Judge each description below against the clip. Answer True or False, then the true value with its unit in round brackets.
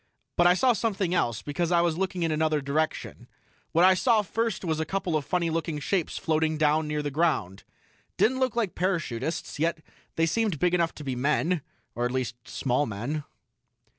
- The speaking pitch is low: False (160 Hz)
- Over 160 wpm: True (195 wpm)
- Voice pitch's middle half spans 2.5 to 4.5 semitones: True (3.5 semitones)